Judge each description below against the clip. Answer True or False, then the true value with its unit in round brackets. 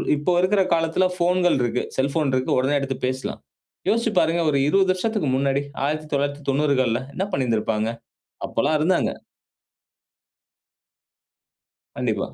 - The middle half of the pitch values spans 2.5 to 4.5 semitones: False (4.9 semitones)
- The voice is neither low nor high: True (145 Hz)